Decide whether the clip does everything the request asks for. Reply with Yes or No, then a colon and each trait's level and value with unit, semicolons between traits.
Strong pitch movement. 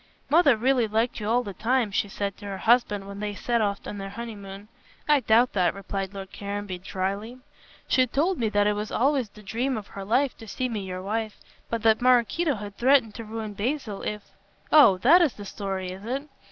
No: average, 3.7 semitones